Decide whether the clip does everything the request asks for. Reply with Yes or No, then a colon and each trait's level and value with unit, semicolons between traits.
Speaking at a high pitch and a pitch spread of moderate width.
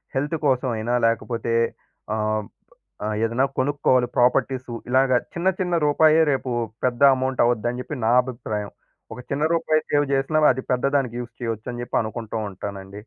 No: low, 125 Hz; average, 3.0 semitones